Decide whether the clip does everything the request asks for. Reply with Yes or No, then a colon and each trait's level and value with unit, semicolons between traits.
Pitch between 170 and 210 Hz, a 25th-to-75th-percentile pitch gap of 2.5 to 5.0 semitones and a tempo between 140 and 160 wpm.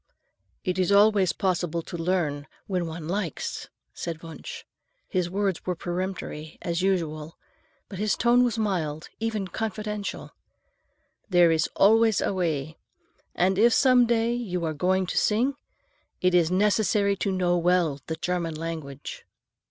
Yes: medium, 185 Hz; average, 4.0 semitones; average, 145 wpm